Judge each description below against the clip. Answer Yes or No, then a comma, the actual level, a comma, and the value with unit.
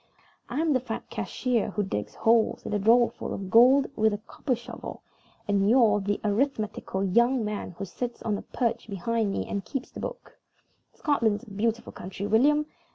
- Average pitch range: Yes, average, 3.4 semitones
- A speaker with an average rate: Yes, average, 175 wpm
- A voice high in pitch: Yes, high, 225 Hz